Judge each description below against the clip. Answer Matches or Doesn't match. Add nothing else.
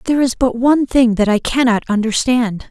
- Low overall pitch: Doesn't match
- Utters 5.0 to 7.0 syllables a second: Matches